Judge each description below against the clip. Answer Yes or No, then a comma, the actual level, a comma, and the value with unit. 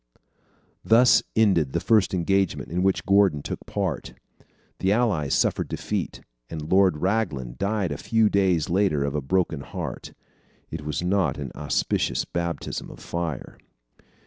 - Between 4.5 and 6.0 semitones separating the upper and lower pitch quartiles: Yes, average, 4.8 semitones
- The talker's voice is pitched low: Yes, very low, 90 Hz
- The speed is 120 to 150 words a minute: Yes, average, 145 wpm